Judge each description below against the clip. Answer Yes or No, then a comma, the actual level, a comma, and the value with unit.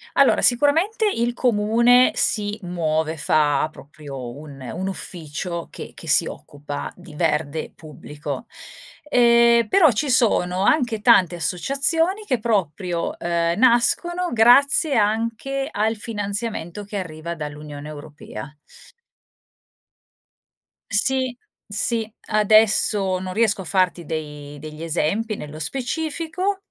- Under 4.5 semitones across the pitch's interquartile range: No, wide, 7.3 semitones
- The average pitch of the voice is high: Yes, high, 205 Hz